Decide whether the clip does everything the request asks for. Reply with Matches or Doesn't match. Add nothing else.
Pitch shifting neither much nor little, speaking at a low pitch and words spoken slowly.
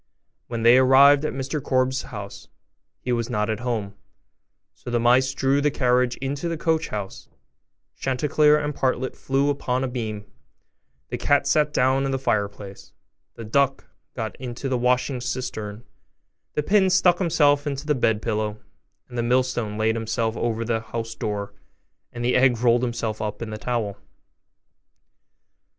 Doesn't match